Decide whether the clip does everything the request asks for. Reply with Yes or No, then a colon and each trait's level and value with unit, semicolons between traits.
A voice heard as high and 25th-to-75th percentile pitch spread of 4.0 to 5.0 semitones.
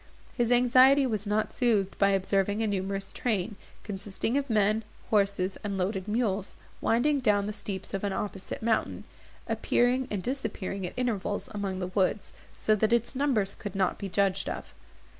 No: high, 205 Hz; average, 3.2 semitones